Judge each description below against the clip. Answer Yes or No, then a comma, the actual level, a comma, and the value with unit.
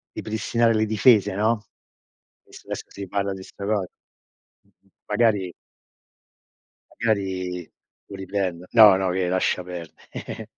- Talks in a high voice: No, low, 100 Hz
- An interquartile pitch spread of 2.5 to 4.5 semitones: Yes, average, 2.8 semitones